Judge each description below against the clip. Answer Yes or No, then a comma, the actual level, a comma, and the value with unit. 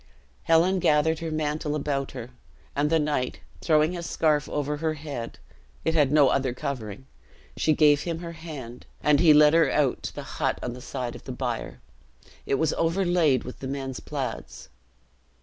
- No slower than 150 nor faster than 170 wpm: No, average, 180 wpm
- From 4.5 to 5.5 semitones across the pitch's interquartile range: No, average, 3.2 semitones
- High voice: No, medium, 150 Hz